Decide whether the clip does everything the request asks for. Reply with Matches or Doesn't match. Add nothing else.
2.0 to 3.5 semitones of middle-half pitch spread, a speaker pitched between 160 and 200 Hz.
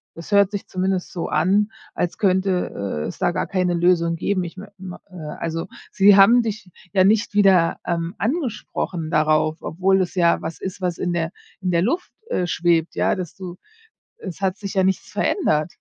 Matches